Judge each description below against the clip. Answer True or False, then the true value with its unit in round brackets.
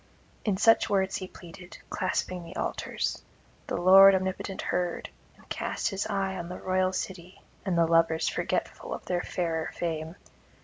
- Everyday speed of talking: True (160 wpm)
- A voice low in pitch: False (185 Hz)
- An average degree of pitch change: False (1.9 semitones)